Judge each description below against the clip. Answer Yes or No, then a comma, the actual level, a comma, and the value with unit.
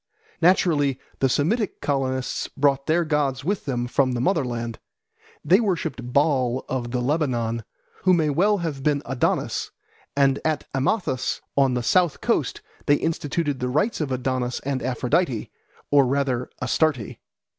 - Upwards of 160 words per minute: No, average, 145 wpm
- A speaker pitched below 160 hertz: Yes, medium, 140 Hz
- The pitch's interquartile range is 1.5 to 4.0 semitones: Yes, average, 3.7 semitones